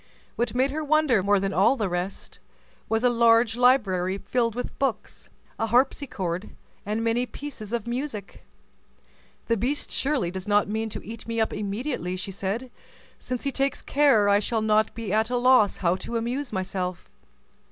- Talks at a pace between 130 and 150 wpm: No, average, 175 wpm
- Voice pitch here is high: Yes, high, 225 Hz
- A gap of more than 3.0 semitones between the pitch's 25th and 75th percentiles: Yes, average, 3.8 semitones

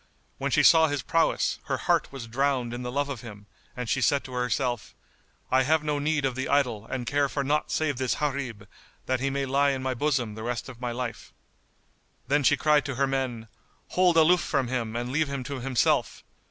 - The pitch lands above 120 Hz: Yes, low, 135 Hz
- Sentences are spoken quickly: Yes, fast, 220 wpm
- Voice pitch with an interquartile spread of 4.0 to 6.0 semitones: No, average, 2.7 semitones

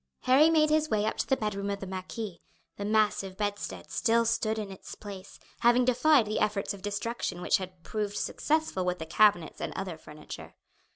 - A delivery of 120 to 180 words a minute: No, average, 190 wpm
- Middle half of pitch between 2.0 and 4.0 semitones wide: Yes, average, 3.4 semitones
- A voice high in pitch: Yes, high, 210 Hz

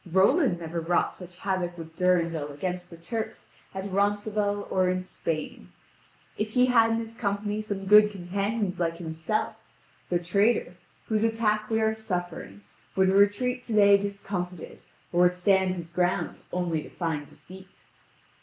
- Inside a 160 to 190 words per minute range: No, average, 150 wpm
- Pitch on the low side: No, high, 190 Hz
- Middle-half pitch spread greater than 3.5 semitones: No, average, 3.2 semitones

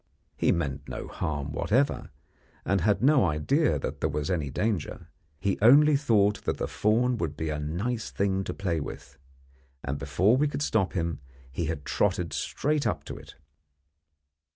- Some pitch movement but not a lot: No, wide, 7.2 semitones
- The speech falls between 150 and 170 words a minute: Yes, average, 165 wpm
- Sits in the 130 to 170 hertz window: No, very low, 95 Hz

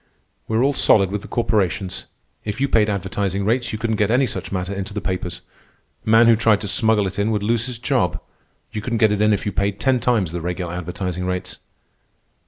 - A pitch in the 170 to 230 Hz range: No, low, 105 Hz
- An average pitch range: Yes, average, 3.1 semitones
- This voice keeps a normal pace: No, fast, 230 wpm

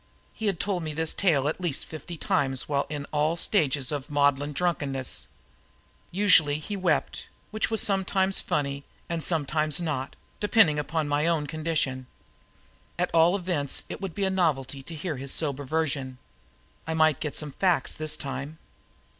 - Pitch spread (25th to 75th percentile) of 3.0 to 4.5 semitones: Yes, average, 3.6 semitones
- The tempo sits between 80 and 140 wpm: No, average, 165 wpm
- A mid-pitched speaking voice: Yes, medium, 155 Hz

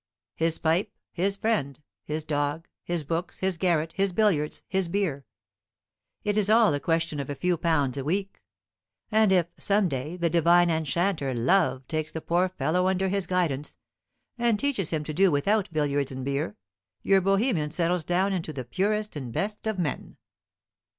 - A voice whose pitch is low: No, medium, 170 Hz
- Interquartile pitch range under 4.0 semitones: No, average, 4.6 semitones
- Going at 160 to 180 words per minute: Yes, average, 170 wpm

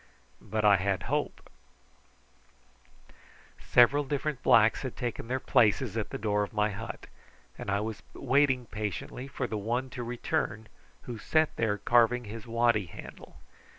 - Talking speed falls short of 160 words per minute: Yes, average, 150 wpm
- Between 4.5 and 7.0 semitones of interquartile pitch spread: No, average, 3.0 semitones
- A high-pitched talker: No, low, 115 Hz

